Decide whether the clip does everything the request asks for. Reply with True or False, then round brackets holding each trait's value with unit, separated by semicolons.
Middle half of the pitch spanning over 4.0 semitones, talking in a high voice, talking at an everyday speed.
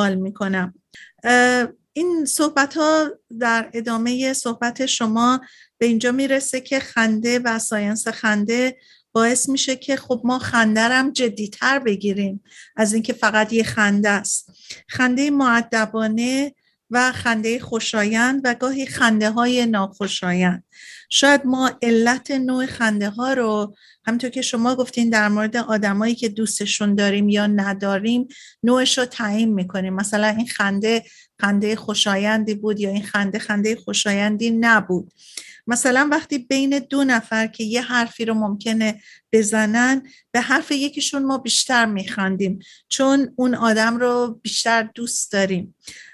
False (3.1 semitones; 230 Hz; 130 wpm)